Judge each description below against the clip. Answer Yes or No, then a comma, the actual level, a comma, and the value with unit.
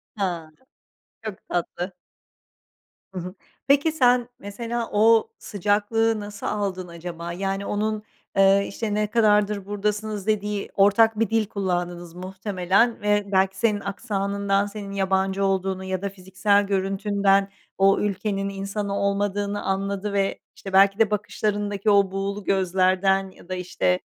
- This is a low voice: No, high, 200 Hz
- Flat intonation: Yes, narrow, 1.5 semitones